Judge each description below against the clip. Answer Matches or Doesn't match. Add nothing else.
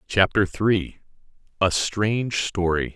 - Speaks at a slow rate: Matches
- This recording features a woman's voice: Doesn't match